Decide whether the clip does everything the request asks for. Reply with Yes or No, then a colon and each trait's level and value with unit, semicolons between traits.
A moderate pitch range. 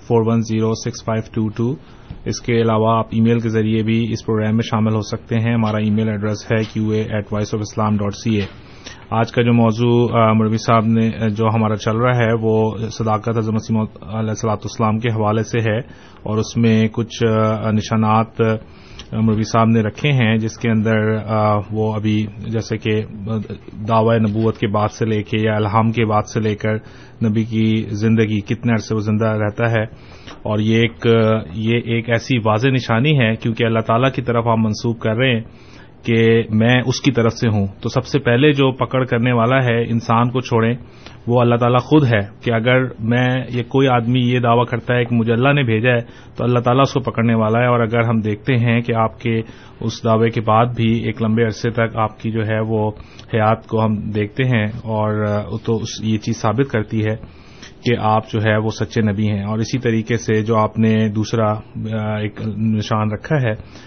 No: narrow, 1.4 semitones